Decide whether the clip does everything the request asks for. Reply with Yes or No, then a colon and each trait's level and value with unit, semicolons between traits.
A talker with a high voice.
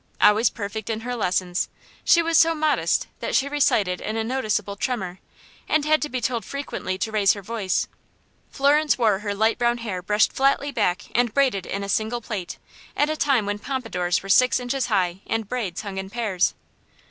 Yes: high, 220 Hz